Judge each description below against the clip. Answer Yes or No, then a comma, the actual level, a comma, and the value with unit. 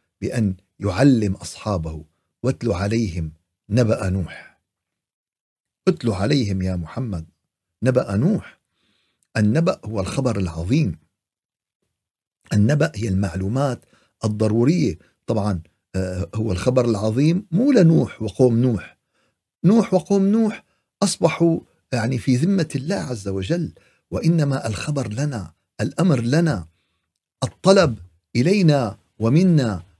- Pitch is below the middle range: Yes, low, 115 Hz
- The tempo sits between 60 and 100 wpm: Yes, average, 95 wpm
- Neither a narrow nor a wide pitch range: No, wide, 7.4 semitones